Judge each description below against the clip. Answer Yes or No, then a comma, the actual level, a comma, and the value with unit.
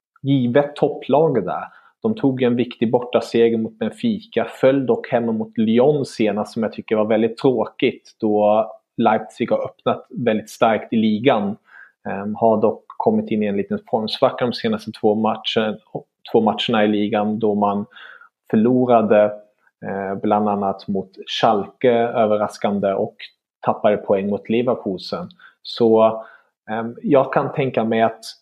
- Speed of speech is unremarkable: Yes, average, 145 wpm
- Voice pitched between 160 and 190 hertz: No, low, 110 Hz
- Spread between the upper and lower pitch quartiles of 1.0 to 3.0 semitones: Yes, narrow, 2.5 semitones